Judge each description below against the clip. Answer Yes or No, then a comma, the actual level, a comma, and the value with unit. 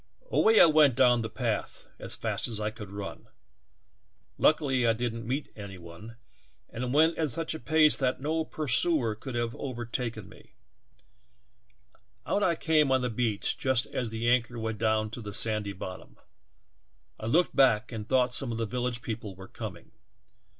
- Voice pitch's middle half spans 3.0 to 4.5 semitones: Yes, average, 3.7 semitones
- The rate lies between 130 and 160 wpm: Yes, average, 145 wpm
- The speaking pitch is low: Yes, low, 120 Hz